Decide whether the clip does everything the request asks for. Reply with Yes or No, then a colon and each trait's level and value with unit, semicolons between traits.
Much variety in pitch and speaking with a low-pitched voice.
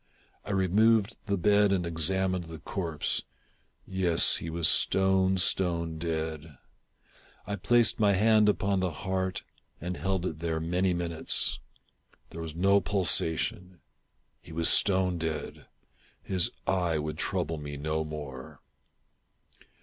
No: average, 2.9 semitones; very low, 90 Hz